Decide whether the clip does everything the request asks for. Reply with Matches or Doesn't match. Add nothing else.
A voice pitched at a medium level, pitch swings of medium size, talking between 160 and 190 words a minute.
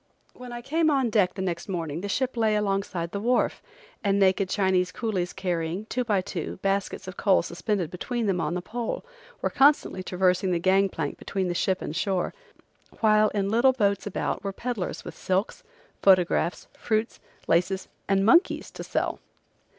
Doesn't match